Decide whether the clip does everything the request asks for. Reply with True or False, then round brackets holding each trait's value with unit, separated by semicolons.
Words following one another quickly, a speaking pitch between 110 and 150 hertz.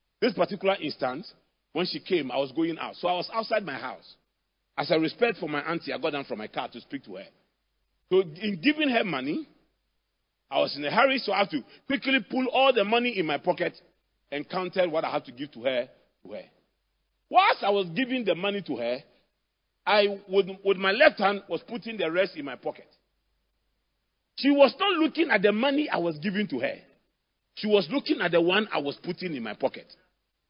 False (215 wpm; 200 Hz)